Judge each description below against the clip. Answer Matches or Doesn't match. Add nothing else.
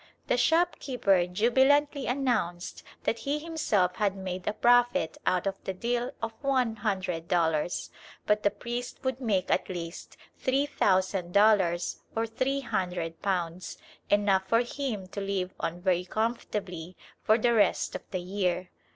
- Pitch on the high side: Matches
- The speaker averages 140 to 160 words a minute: Matches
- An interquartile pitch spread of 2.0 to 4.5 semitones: Doesn't match